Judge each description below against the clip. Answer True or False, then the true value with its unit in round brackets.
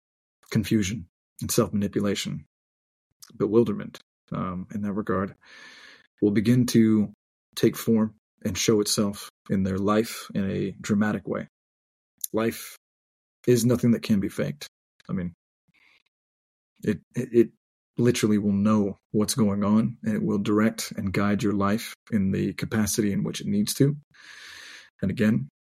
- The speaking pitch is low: True (105 Hz)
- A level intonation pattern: True (2.3 semitones)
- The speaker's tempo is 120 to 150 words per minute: True (140 wpm)